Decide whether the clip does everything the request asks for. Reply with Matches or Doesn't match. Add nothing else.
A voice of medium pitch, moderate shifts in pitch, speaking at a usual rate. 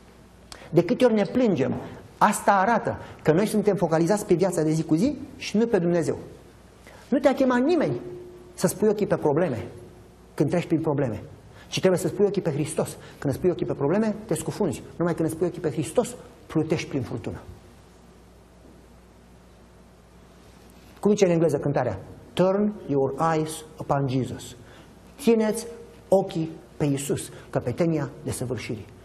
Doesn't match